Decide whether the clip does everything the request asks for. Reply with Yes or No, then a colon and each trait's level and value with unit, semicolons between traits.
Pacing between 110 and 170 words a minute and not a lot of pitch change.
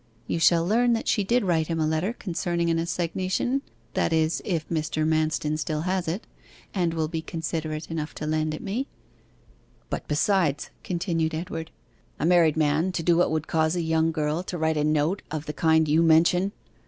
No: average, 190 wpm; narrow, 2.1 semitones